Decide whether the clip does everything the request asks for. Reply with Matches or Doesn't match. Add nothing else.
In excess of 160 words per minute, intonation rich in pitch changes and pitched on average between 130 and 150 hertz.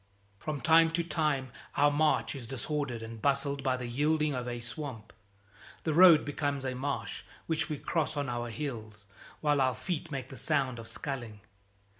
Doesn't match